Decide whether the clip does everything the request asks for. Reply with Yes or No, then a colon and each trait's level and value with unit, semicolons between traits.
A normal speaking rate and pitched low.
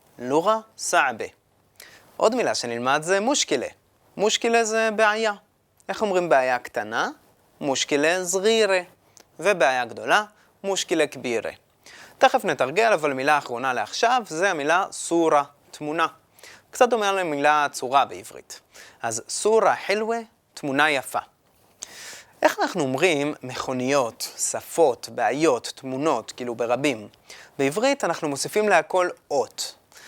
No: average, 110 wpm; medium, 160 Hz